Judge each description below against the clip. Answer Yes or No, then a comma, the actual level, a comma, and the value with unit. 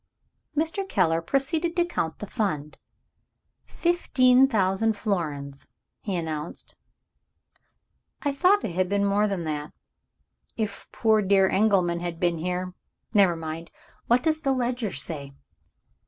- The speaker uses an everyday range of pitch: No, wide, 7.0 semitones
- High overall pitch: Yes, high, 200 Hz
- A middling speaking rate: No, slow, 125 wpm